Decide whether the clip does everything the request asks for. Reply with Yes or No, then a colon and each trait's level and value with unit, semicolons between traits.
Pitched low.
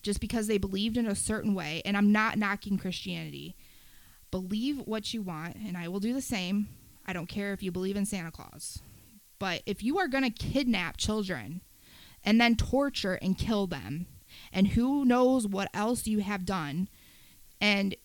No: high, 200 Hz